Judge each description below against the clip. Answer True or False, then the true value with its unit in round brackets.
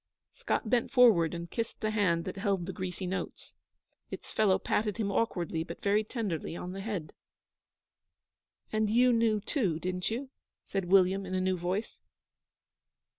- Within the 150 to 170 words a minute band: True (160 wpm)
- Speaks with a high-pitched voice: True (195 Hz)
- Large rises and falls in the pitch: False (3.2 semitones)